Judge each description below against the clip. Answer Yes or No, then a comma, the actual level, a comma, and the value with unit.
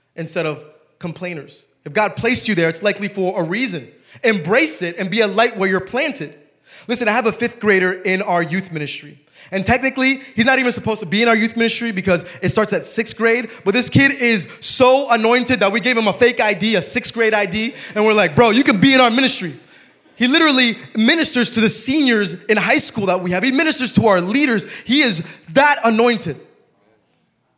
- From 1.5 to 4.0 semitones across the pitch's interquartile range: No, average, 4.8 semitones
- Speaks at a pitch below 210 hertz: No, high, 220 Hz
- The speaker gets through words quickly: Yes, fast, 215 wpm